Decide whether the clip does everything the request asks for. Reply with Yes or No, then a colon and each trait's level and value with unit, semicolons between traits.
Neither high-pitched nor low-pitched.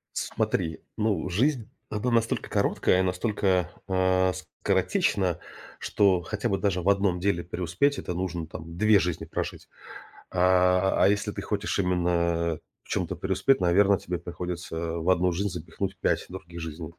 No: very low, 90 Hz